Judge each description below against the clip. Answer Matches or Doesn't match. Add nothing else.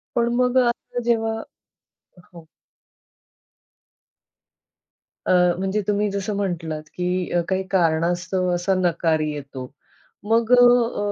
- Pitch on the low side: Doesn't match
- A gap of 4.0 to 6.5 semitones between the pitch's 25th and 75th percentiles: Matches